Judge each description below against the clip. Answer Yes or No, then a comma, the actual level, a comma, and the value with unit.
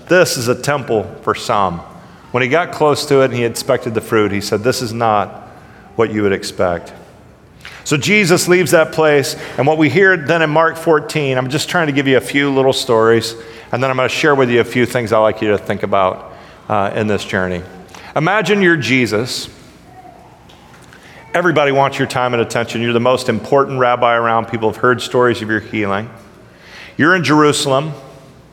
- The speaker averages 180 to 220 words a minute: Yes, average, 200 wpm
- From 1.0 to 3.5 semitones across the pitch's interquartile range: No, average, 4.8 semitones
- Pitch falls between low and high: No, low, 130 Hz